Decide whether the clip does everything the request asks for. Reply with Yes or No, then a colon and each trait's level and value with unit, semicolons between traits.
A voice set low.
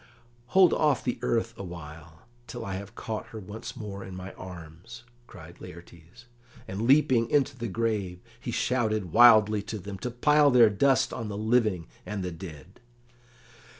Yes: low, 105 Hz